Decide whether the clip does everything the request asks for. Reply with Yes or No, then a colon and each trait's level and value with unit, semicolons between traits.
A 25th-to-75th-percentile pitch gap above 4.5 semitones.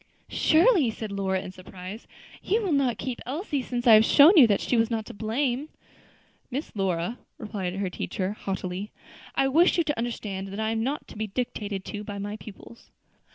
Yes: average, 5.0 semitones